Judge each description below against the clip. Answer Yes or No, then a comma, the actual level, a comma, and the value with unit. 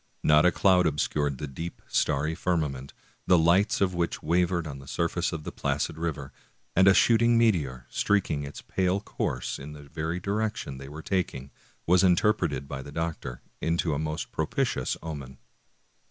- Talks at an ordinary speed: Yes, average, 170 wpm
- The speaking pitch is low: Yes, very low, 80 Hz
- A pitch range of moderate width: Yes, average, 4.1 semitones